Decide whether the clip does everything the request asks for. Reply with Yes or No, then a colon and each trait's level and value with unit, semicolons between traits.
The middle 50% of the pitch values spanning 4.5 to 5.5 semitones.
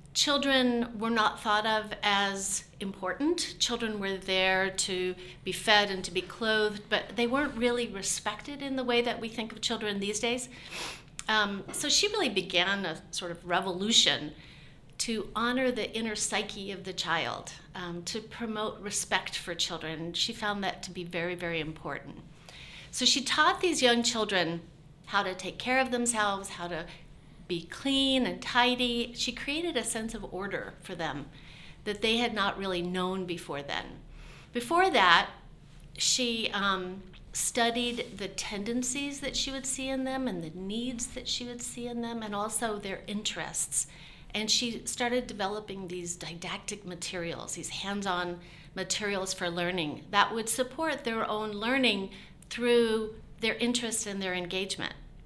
Yes: average, 4.8 semitones